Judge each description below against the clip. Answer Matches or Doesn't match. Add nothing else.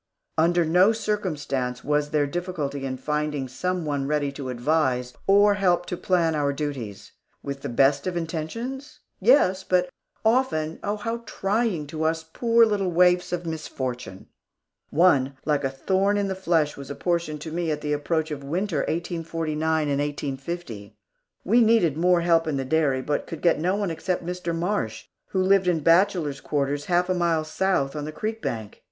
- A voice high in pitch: Doesn't match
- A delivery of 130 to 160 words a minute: Doesn't match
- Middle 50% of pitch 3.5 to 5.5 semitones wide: Matches